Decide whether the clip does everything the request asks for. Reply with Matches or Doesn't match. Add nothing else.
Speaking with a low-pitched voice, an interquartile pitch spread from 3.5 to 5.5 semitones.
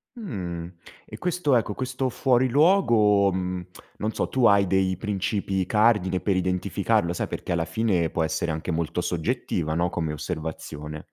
Matches